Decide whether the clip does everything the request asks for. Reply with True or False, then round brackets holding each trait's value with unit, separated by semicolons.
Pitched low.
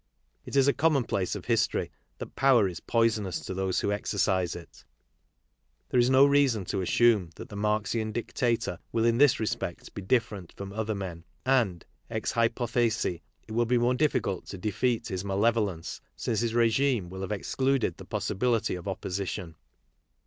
True (110 Hz)